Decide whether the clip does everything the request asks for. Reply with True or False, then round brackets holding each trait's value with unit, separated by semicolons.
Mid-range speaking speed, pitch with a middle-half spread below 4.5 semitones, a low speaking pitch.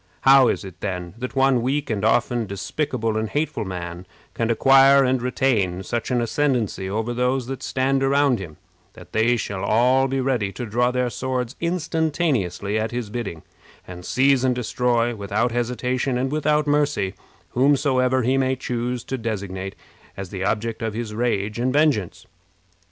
True (165 wpm; 3.9 semitones; 120 Hz)